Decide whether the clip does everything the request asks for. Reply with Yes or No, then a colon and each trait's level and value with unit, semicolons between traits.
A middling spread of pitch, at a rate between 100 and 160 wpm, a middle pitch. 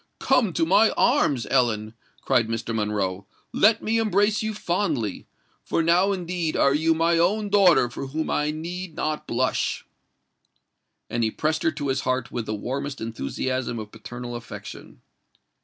No: wide, 7.1 semitones; average, 155 wpm; medium, 150 Hz